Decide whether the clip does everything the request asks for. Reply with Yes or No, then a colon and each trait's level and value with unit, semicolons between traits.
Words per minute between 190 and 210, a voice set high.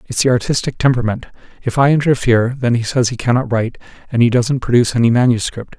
No: average, 195 wpm; low, 125 Hz